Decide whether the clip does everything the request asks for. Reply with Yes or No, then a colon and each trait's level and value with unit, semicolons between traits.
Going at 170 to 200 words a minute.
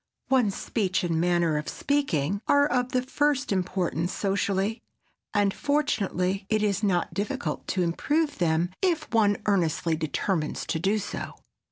No: average, 145 wpm